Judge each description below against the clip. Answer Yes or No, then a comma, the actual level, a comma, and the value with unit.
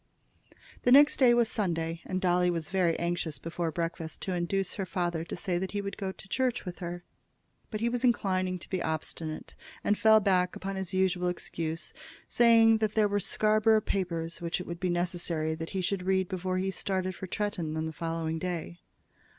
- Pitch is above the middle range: No, medium, 180 Hz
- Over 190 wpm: Yes, average, 200 wpm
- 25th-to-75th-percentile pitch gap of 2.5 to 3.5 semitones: Yes, average, 2.8 semitones